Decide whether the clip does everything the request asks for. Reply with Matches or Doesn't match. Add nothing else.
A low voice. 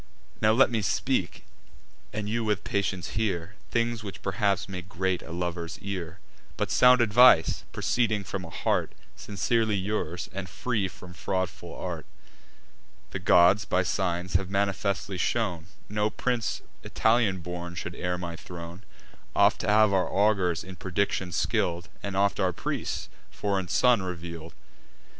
Matches